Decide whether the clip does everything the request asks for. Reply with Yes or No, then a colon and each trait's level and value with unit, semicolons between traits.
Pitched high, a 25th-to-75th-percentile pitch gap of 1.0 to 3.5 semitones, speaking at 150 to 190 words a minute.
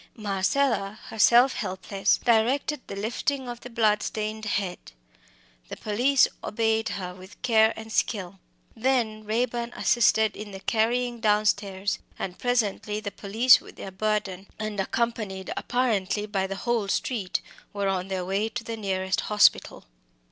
No: high, 215 Hz; average, 3.1 semitones; average, 140 wpm